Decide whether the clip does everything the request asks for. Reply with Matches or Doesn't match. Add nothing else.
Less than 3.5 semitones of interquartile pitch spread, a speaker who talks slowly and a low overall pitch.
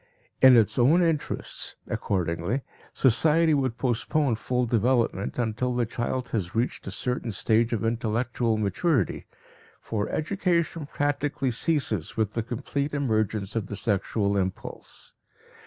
Doesn't match